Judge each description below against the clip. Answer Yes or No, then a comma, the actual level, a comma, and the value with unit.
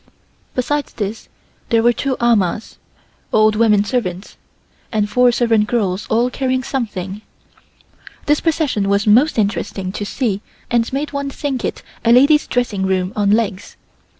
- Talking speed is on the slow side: No, average, 145 wpm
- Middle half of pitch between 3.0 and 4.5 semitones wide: Yes, average, 3.9 semitones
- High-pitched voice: Yes, high, 230 Hz